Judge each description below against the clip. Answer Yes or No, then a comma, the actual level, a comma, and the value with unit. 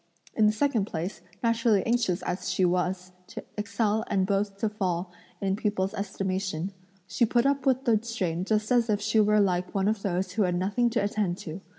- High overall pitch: Yes, high, 200 Hz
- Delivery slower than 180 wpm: No, average, 200 wpm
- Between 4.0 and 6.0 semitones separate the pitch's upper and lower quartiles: No, average, 2.9 semitones